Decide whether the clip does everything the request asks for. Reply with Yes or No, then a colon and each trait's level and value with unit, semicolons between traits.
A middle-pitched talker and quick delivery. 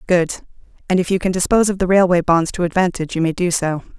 Yes: medium, 180 Hz; fast, 240 wpm